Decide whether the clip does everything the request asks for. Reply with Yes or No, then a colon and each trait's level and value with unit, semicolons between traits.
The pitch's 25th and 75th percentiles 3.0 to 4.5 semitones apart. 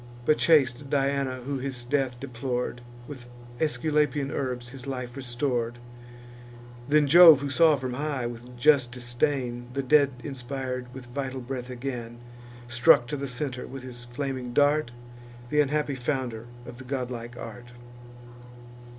No: narrow, 2.5 semitones